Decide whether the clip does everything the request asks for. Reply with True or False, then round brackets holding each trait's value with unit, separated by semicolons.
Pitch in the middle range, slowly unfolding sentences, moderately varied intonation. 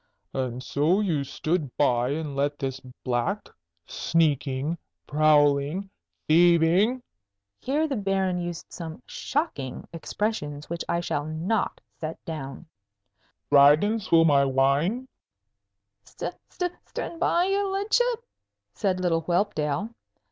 False (165 Hz; 110 wpm; 6.0 semitones)